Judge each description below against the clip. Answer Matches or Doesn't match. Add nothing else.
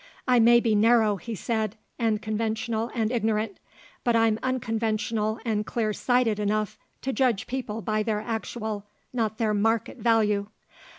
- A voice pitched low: Doesn't match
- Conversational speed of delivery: Matches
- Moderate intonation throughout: Doesn't match